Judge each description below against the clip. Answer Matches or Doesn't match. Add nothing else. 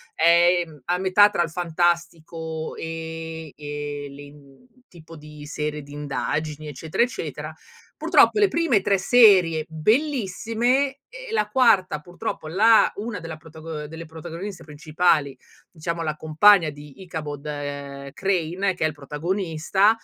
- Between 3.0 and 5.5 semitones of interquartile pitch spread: Matches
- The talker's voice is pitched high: Doesn't match